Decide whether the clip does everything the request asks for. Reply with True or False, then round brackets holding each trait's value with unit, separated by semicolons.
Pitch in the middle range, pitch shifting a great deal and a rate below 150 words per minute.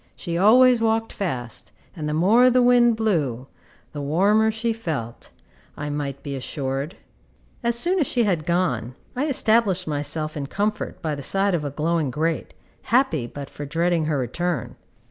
False (170 Hz; 7.3 semitones; 165 wpm)